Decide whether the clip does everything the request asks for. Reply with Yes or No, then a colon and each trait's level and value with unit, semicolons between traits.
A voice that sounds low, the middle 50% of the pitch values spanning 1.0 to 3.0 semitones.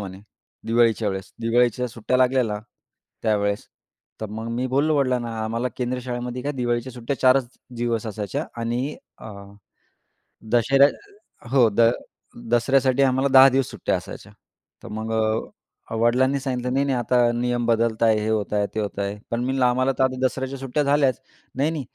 Yes: low, 120 Hz; narrow, 2.5 semitones